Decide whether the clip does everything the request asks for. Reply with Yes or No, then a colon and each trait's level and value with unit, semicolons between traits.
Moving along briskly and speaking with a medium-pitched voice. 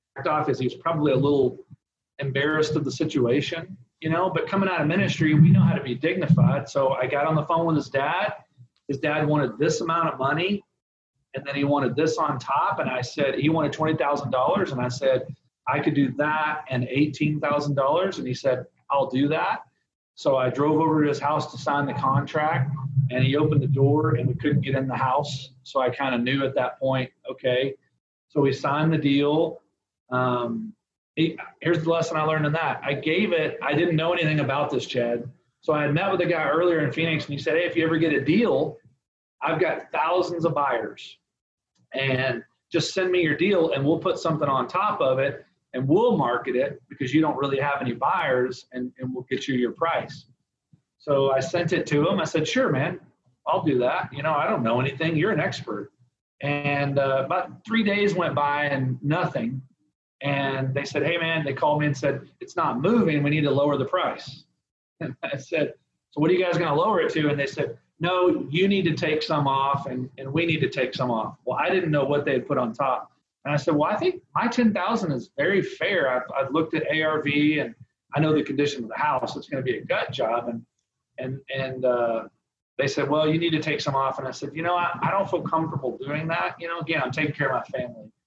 Yes: fast, 230 wpm; medium, 145 Hz